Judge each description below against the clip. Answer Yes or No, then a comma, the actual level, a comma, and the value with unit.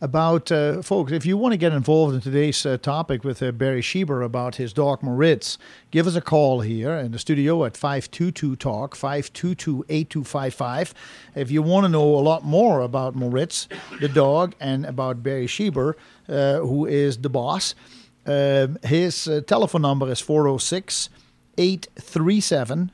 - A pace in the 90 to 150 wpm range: No, average, 165 wpm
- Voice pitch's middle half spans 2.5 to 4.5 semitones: Yes, average, 3.6 semitones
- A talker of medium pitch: Yes, medium, 145 Hz